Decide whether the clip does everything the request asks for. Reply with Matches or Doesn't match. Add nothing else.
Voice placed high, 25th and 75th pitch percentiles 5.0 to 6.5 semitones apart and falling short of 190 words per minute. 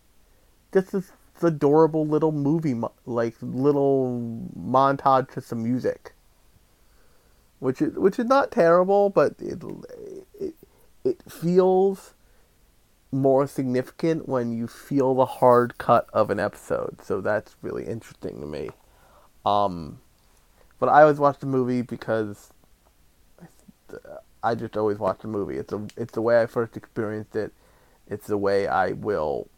Doesn't match